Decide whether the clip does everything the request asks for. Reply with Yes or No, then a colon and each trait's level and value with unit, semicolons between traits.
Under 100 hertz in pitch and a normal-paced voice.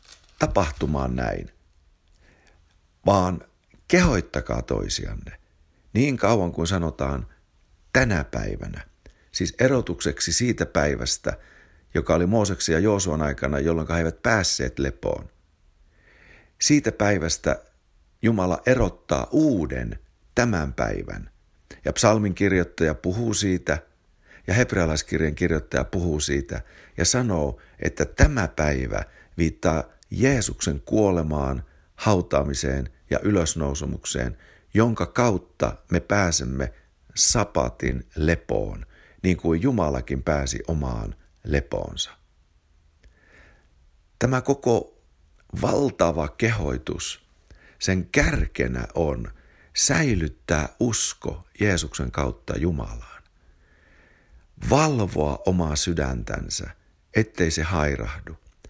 No: very low, 80 Hz; slow, 85 wpm